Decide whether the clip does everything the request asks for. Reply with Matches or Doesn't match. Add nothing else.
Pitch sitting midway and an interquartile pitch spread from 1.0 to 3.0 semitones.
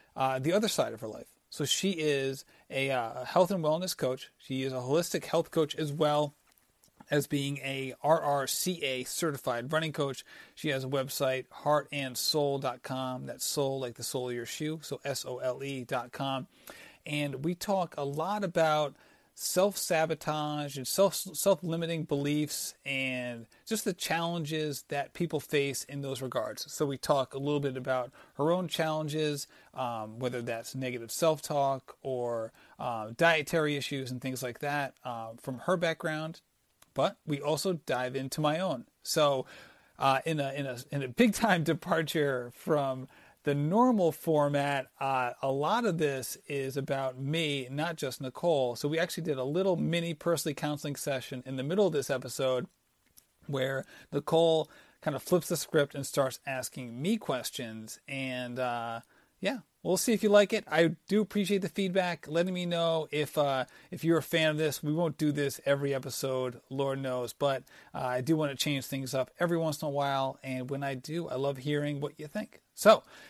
Doesn't match